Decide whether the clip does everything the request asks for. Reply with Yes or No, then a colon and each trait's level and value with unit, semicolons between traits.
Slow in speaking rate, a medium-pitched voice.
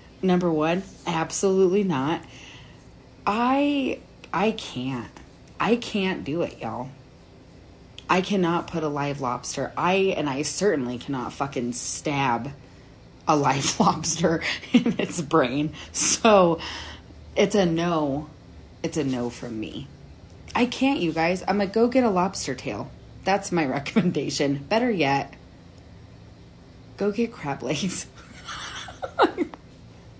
Yes: slow, 120 wpm; medium, 165 Hz